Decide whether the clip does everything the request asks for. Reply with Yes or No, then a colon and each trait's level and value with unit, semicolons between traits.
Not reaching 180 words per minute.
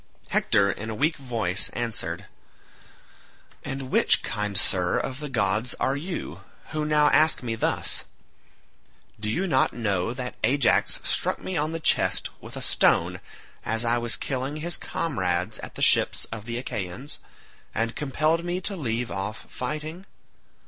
Yes: average, 155 wpm